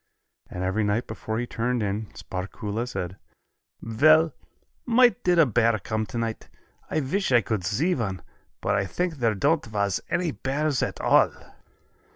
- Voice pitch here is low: Yes, low, 115 Hz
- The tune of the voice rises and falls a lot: Yes, wide, 7.1 semitones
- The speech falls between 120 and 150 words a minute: No, average, 160 wpm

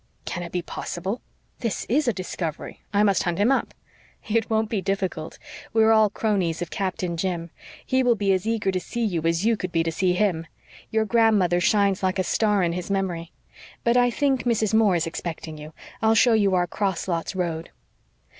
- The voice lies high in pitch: Yes, high, 195 Hz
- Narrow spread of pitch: No, average, 4.1 semitones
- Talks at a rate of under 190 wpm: No, fast, 205 wpm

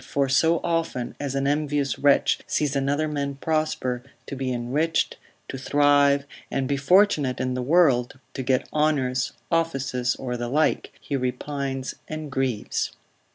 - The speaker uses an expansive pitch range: No, average, 2.7 semitones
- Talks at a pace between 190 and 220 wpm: No, average, 150 wpm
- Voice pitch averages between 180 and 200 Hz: No, medium, 140 Hz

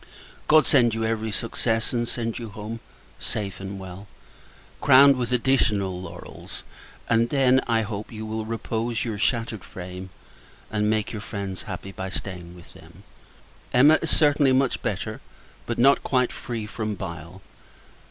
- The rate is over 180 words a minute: No, average, 155 wpm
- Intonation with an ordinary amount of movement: Yes, average, 3.5 semitones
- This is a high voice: No, low, 110 Hz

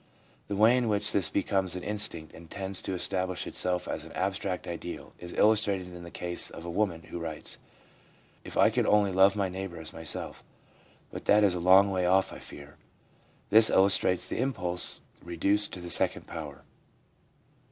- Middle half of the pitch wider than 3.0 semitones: No, narrow, 2.5 semitones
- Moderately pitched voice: No, very low, 95 Hz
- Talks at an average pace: Yes, average, 190 wpm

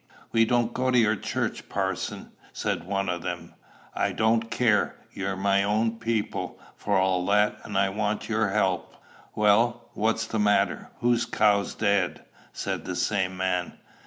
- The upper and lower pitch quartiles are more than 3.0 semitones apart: No, narrow, 2.6 semitones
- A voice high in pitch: No, low, 105 Hz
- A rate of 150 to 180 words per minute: Yes, average, 160 wpm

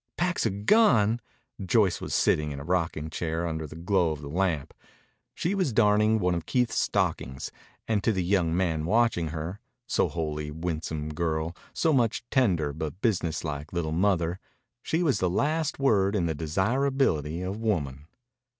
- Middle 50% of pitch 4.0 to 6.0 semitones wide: Yes, wide, 5.6 semitones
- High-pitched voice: No, very low, 90 Hz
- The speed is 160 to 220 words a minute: Yes, average, 170 wpm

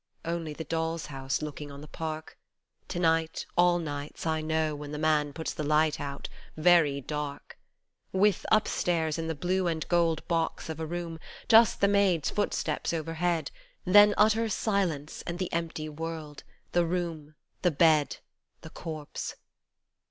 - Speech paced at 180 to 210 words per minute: No, average, 155 wpm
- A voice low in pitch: No, medium, 160 Hz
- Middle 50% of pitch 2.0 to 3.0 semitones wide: Yes, narrow, 2.4 semitones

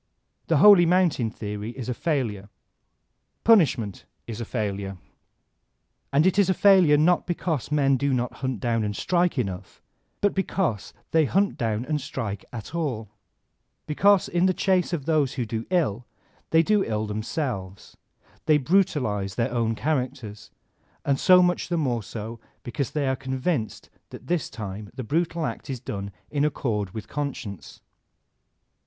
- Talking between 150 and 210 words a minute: Yes, average, 160 wpm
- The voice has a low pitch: Yes, low, 130 Hz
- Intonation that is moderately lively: No, wide, 7.2 semitones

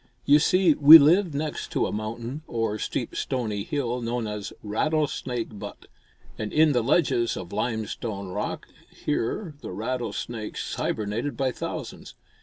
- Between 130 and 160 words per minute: Yes, average, 140 wpm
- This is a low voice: Yes, low, 120 Hz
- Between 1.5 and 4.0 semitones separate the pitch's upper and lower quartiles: No, average, 5.3 semitones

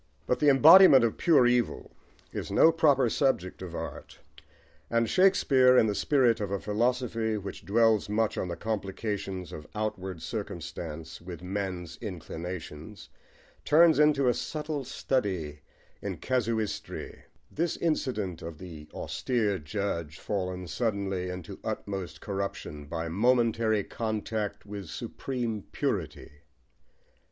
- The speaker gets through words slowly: Yes, slow, 125 wpm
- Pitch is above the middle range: No, low, 105 Hz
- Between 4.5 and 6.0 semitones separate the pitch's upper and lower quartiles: Yes, average, 5.2 semitones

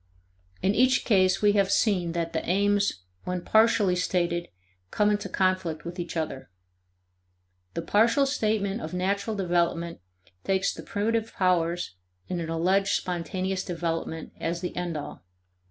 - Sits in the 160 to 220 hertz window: Yes, medium, 185 Hz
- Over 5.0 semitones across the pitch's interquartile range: No, average, 2.9 semitones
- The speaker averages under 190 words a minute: Yes, average, 140 wpm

